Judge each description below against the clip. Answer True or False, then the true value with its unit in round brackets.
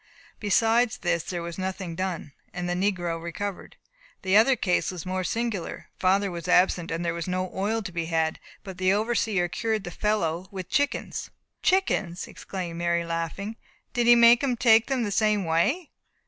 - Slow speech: False (175 wpm)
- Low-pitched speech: False (185 Hz)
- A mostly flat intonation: False (4.2 semitones)